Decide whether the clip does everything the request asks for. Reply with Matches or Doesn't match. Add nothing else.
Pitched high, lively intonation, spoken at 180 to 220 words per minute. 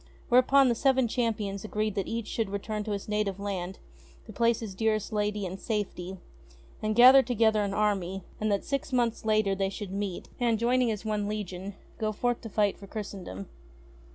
Doesn't match